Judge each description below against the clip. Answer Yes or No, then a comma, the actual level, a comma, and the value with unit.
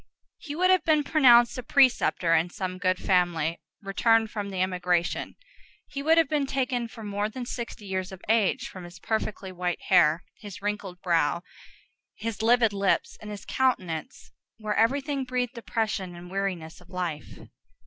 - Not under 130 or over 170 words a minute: Yes, average, 165 wpm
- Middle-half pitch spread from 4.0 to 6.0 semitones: Yes, average, 5.1 semitones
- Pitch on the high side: Yes, high, 205 Hz